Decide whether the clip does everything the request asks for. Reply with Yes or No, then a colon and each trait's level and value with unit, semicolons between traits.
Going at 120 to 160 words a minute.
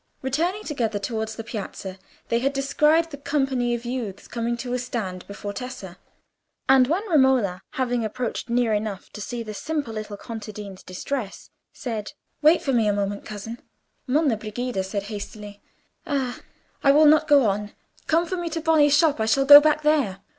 No: average, 175 wpm